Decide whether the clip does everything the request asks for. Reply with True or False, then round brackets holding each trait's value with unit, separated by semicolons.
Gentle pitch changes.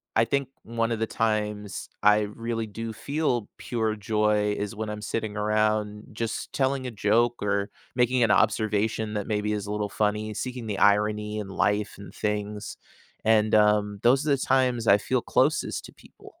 True (1.7 semitones)